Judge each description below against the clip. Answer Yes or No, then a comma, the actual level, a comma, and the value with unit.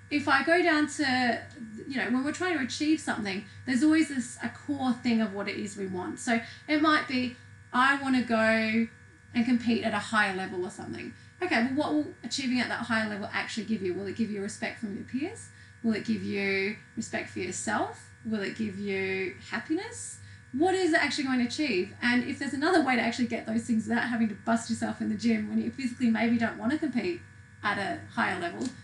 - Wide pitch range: No, average, 4.2 semitones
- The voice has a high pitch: Yes, high, 235 Hz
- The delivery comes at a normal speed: No, fast, 230 wpm